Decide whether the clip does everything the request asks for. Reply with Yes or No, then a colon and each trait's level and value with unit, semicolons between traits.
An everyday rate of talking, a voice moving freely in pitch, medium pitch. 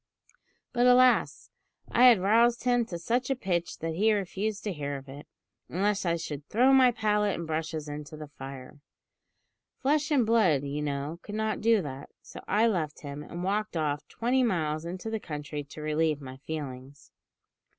Yes: average, 180 wpm; wide, 6.9 semitones; medium, 170 Hz